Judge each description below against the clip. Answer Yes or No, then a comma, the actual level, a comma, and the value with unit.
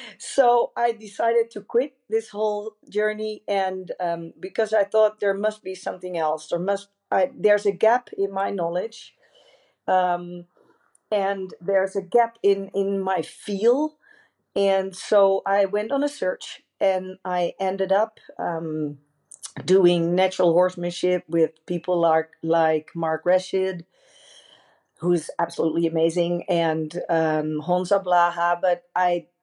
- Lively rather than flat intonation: No, average, 3.2 semitones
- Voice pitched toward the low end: No, high, 190 Hz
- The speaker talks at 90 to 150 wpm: Yes, slow, 135 wpm